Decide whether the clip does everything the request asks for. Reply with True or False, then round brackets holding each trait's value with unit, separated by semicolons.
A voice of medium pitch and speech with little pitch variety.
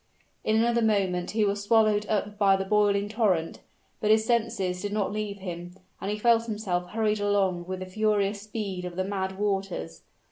False (205 Hz; 2.3 semitones)